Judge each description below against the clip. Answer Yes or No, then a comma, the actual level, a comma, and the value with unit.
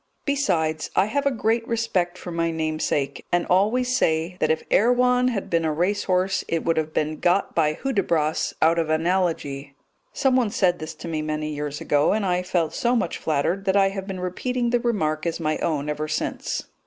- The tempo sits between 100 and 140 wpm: No, average, 195 wpm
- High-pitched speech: No, medium, 175 Hz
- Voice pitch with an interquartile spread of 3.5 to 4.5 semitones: No, average, 5.0 semitones